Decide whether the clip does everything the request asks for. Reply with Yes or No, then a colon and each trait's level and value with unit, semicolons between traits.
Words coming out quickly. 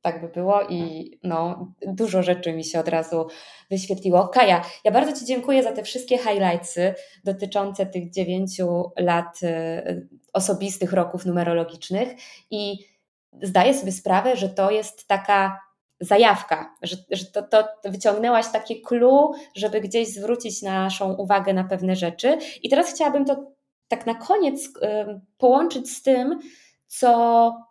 No: average, 135 wpm